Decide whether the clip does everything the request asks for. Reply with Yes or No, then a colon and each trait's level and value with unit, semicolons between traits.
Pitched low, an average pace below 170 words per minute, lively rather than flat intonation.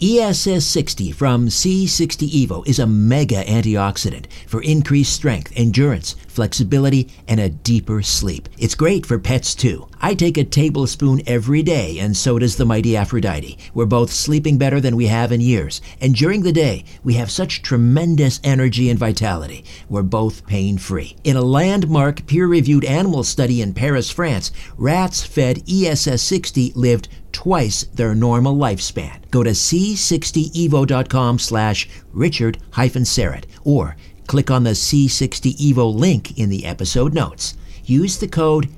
Yes: low, 125 Hz; average, 145 wpm; wide, 5.7 semitones